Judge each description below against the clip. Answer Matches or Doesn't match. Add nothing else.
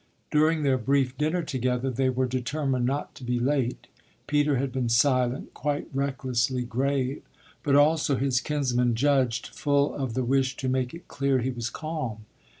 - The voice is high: Doesn't match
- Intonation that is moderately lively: Doesn't match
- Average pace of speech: Matches